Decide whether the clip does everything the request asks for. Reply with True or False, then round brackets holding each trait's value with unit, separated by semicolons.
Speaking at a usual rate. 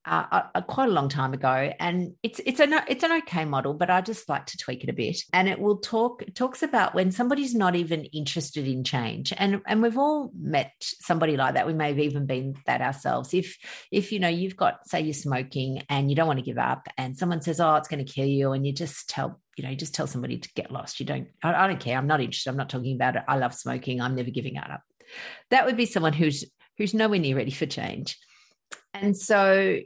False (250 wpm)